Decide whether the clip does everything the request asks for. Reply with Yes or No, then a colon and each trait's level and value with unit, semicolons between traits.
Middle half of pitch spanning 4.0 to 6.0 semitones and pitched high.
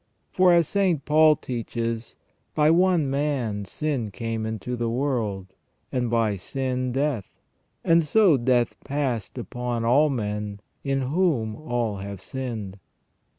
No: average, 4.9 semitones; low, 125 Hz